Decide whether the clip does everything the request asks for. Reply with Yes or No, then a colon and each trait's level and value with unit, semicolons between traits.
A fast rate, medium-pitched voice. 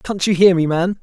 Yes: fast, 295 wpm; medium, 180 Hz